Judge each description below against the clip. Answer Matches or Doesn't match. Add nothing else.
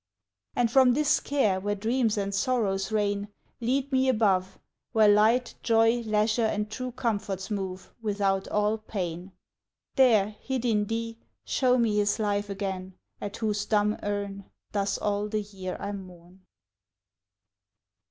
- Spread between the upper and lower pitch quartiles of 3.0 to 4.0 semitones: Doesn't match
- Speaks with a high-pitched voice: Matches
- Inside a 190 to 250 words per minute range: Doesn't match